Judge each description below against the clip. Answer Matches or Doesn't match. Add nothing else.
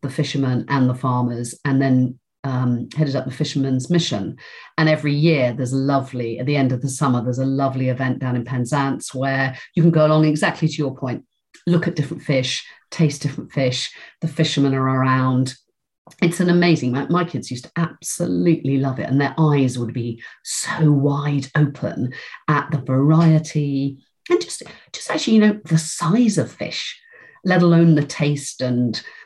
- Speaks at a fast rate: Doesn't match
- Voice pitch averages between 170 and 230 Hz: Doesn't match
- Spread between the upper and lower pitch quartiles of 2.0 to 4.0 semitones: Matches